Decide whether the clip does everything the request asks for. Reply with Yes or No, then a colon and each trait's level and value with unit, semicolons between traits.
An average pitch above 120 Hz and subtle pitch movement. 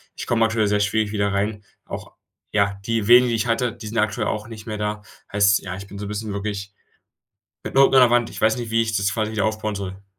No: low, 105 Hz; narrow, 1.9 semitones